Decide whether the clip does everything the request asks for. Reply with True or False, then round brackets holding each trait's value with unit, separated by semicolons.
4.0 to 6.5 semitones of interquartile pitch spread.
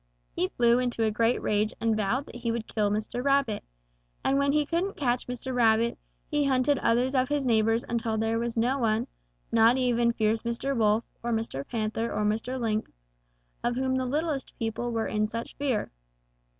False (2.6 semitones)